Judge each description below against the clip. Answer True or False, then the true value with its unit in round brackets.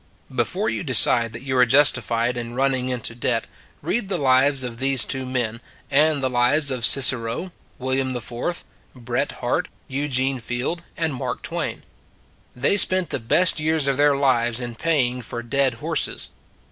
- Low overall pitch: True (130 Hz)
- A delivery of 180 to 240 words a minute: False (160 wpm)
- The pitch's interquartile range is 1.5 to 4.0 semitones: True (2.8 semitones)